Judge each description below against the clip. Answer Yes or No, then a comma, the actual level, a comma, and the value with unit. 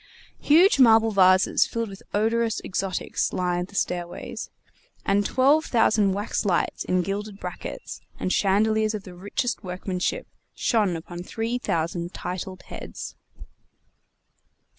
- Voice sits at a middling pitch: No, high, 200 Hz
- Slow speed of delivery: Yes, slow, 120 wpm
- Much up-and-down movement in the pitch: No, average, 3.5 semitones